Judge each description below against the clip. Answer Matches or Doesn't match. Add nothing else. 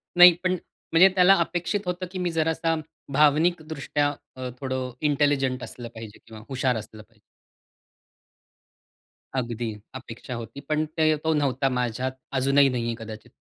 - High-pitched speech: Doesn't match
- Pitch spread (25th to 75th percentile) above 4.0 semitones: Matches